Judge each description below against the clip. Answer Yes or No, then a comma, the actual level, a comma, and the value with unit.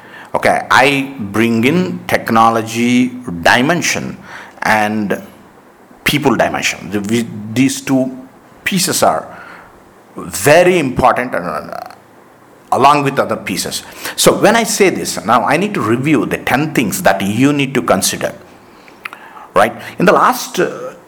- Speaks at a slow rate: Yes, slow, 130 wpm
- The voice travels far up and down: No, average, 3.8 semitones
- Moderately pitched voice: No, low, 120 Hz